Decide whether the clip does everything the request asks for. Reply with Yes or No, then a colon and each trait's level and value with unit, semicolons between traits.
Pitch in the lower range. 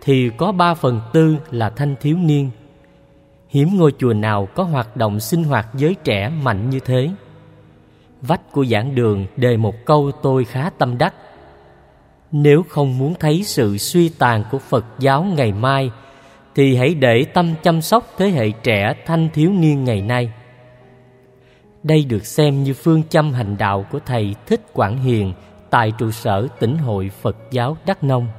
Yes: low, 130 Hz